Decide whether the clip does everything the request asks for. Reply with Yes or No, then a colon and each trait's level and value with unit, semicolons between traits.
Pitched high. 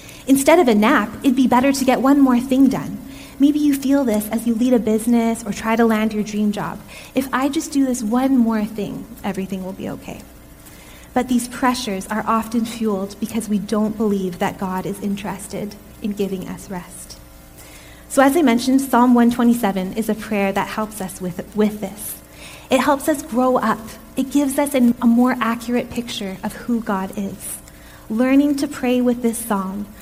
Yes: high, 225 Hz